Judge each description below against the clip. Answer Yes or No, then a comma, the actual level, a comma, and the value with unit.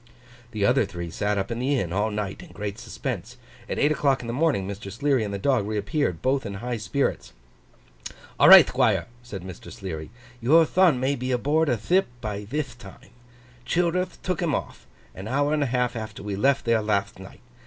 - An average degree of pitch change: No, wide, 5.7 semitones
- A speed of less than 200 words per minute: No, fast, 205 wpm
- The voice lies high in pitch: No, low, 115 Hz